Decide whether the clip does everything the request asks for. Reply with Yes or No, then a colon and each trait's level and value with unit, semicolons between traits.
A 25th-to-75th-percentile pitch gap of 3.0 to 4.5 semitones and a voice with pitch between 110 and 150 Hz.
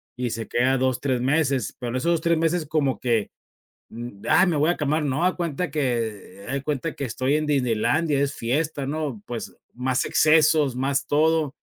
Yes: average, 3.8 semitones; medium, 140 Hz